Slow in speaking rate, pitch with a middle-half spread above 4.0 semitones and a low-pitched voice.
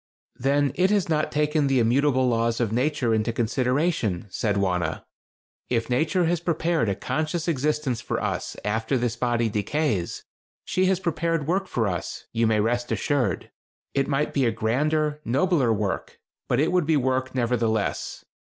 No: average, 160 wpm; average, 5.2 semitones; low, 130 Hz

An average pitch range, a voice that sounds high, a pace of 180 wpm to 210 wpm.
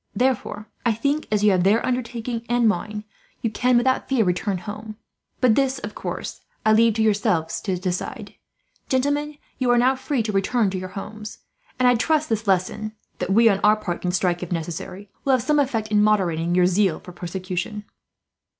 Yes: average, 4.7 semitones; high, 215 Hz; average, 195 wpm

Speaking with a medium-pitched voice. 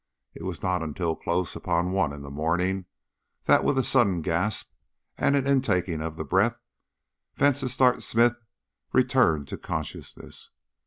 No: very low, 90 Hz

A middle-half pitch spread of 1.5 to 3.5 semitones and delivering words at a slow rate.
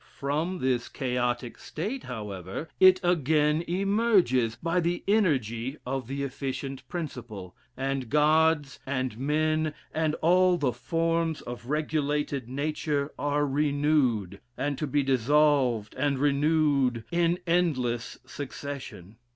No: average, 3.9 semitones; slow, 115 wpm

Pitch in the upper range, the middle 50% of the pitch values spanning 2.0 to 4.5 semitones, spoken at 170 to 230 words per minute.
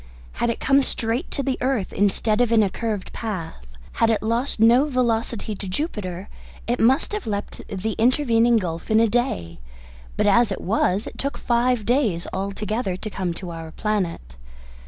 Yes: high, 220 Hz; average, 3.8 semitones; average, 180 wpm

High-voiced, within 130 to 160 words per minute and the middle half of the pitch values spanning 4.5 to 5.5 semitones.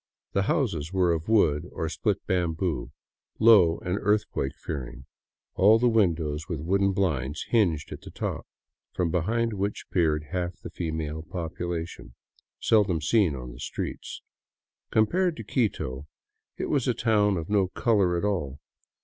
No: very low, 90 Hz; average, 150 wpm; average, 4.8 semitones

